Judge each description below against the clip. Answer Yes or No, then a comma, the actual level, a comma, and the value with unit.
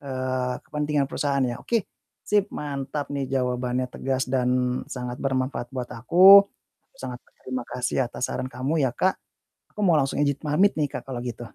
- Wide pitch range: No, average, 3.0 semitones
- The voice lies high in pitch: No, low, 135 Hz